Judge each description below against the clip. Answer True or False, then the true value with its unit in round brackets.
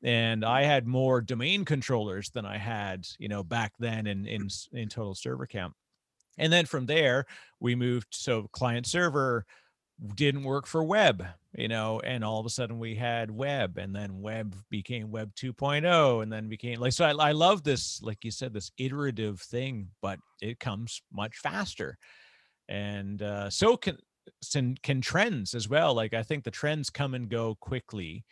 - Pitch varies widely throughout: False (4.3 semitones)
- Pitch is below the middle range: True (120 Hz)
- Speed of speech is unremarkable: True (180 wpm)